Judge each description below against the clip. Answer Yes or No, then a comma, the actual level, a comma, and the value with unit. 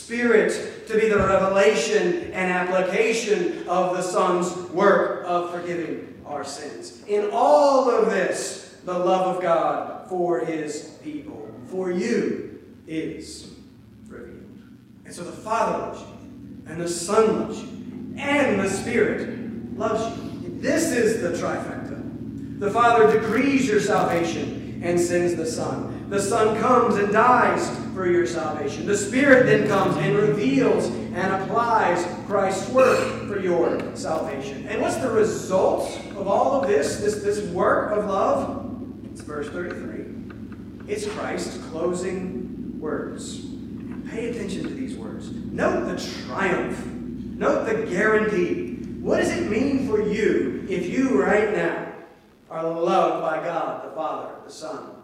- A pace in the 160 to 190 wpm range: No, average, 140 wpm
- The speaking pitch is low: No, high, 205 Hz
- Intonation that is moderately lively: Yes, average, 4.6 semitones